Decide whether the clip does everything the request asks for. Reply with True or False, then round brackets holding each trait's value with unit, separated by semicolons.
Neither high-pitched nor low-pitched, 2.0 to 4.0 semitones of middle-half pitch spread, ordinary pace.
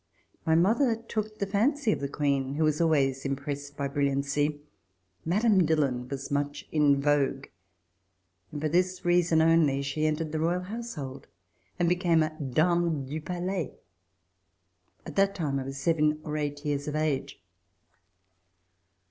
True (155 Hz; 3.7 semitones; 150 wpm)